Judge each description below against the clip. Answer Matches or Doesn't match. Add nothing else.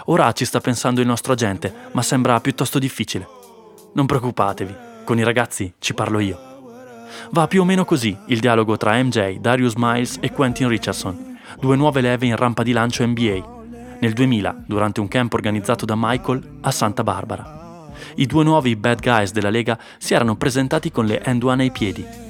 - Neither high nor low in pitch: Doesn't match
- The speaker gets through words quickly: Matches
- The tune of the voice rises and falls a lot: Doesn't match